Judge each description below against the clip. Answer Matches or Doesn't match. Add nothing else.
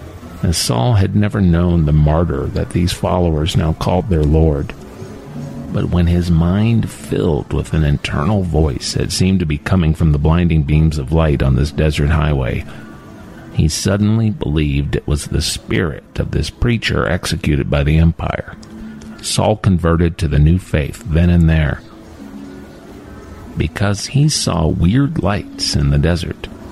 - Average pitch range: Matches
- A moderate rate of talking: Matches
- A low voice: Matches